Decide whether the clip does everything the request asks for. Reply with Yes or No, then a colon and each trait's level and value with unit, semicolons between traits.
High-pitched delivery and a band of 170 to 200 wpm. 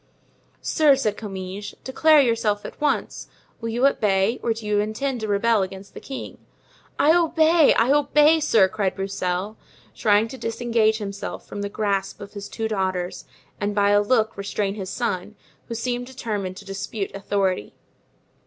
No: high, 215 Hz; average, 160 wpm